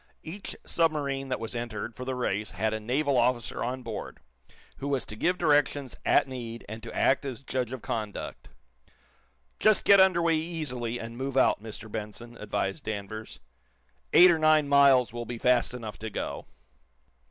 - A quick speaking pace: No, average, 175 wpm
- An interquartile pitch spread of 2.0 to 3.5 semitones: No, average, 4.0 semitones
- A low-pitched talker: Yes, low, 125 Hz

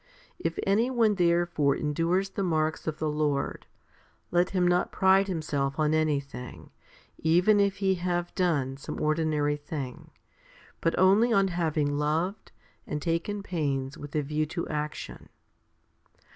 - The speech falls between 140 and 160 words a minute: Yes, average, 145 wpm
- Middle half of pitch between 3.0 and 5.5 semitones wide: Yes, average, 3.9 semitones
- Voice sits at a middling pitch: Yes, medium, 165 Hz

